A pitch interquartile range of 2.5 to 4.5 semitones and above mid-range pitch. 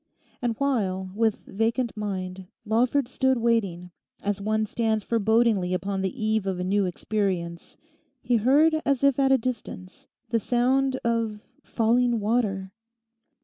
Yes: average, 3.9 semitones; high, 220 Hz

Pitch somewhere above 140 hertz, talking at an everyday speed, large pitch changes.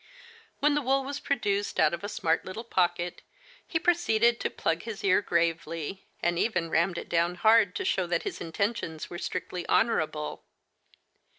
No: medium, 185 Hz; average, 170 wpm; average, 5.0 semitones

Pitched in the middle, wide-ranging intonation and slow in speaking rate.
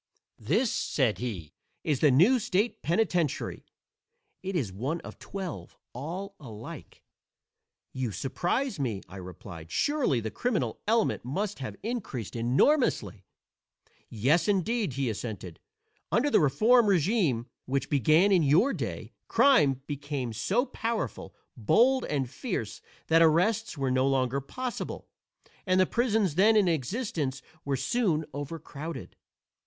Yes: medium, 155 Hz; wide, 8.5 semitones; slow, 125 wpm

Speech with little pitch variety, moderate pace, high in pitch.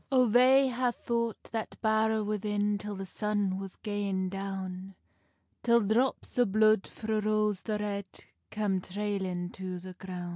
Yes: narrow, 2.3 semitones; average, 150 wpm; high, 210 Hz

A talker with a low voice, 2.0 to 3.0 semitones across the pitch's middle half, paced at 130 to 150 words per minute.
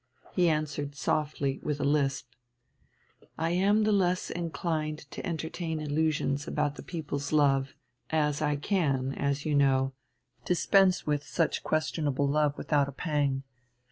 No: medium, 150 Hz; narrow, 2.4 semitones; average, 140 wpm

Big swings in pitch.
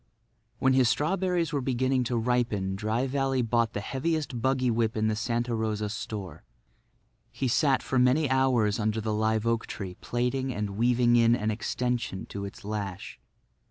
No: average, 3.3 semitones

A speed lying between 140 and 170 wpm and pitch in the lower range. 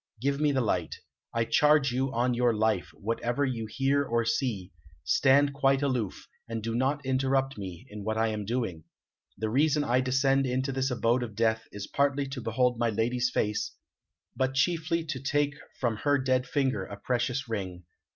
No: average, 180 wpm; low, 125 Hz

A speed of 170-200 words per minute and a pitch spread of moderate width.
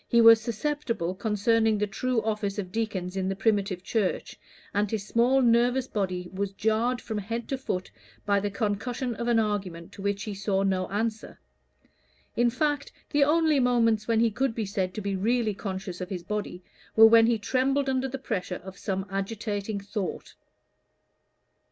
Yes: average, 175 wpm; average, 3.2 semitones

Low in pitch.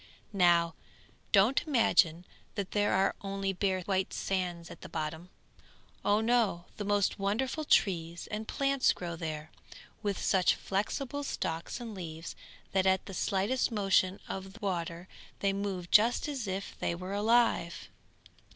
No: high, 195 Hz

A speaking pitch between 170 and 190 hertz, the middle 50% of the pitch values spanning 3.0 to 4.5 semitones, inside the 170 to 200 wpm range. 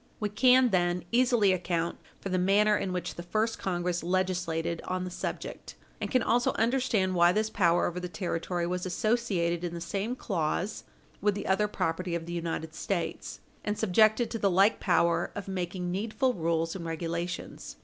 Yes: medium, 185 Hz; average, 3.5 semitones; average, 180 wpm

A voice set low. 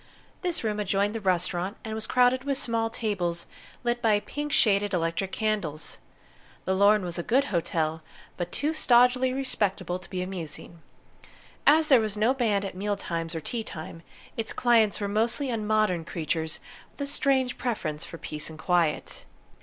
No: high, 205 Hz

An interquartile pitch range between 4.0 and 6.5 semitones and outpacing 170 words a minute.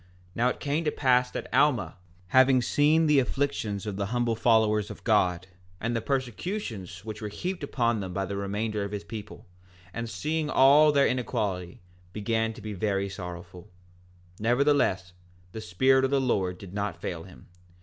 Yes: average, 5.2 semitones; average, 180 wpm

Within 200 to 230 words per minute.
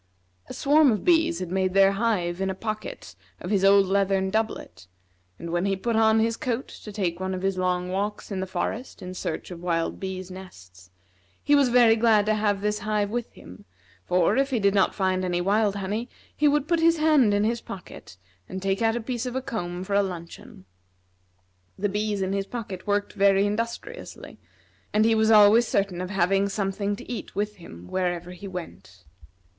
Yes: fast, 205 wpm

